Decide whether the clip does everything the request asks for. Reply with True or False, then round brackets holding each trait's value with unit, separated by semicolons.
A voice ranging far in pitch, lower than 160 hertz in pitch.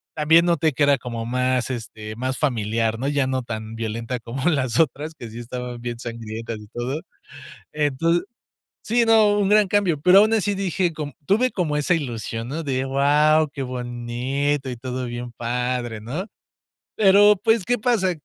True (5.7 semitones; 135 Hz)